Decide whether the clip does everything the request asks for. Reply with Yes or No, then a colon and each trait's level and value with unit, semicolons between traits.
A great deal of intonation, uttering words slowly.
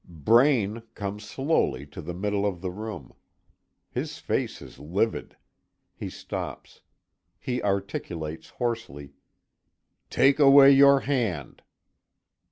Yes: wide, 6.6 semitones; slow, 105 wpm